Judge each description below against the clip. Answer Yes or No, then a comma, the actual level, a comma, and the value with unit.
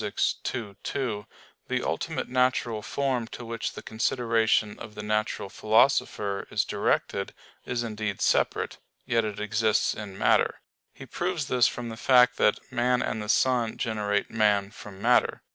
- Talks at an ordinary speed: Yes, average, 150 wpm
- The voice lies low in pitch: Yes, low, 110 Hz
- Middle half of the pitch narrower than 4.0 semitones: Yes, average, 2.8 semitones